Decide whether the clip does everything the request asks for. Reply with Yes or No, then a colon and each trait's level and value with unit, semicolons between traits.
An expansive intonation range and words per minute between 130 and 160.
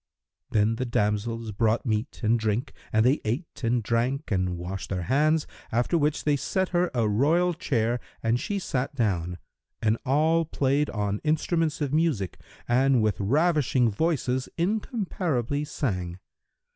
Yes: wide, 5.9 semitones; average, 145 wpm